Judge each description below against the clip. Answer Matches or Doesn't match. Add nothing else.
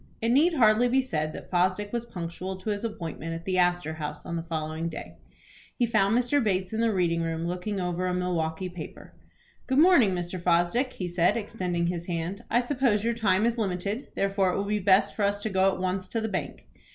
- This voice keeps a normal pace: Doesn't match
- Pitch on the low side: Doesn't match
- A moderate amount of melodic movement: Matches